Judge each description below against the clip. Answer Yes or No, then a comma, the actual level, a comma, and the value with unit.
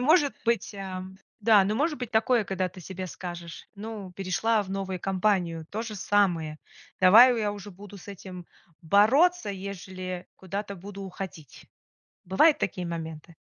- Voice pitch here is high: Yes, high, 195 Hz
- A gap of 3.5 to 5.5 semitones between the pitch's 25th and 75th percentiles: No, average, 2.7 semitones